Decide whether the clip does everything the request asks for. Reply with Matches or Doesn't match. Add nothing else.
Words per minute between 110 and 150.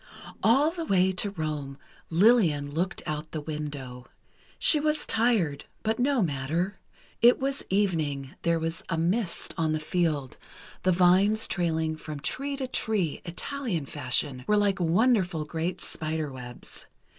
Matches